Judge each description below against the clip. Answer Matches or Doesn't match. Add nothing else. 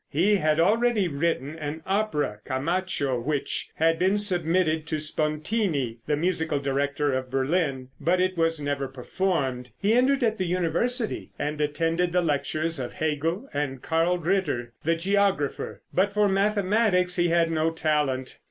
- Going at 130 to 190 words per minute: Matches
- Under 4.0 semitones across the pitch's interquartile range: Doesn't match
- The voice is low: Doesn't match